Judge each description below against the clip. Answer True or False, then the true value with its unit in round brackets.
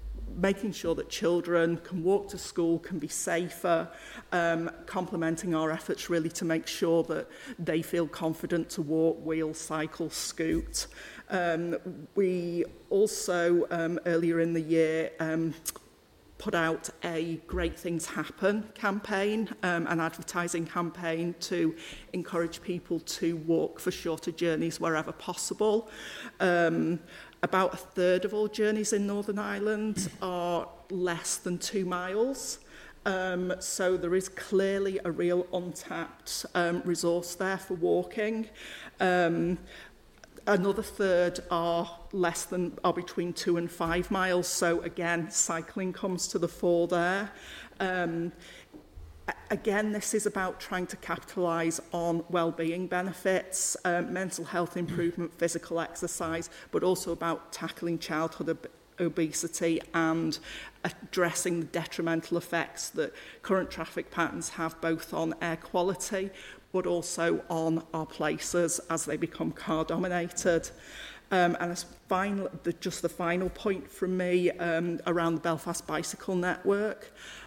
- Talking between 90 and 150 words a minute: True (135 wpm)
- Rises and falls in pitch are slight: True (1.9 semitones)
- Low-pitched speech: False (175 Hz)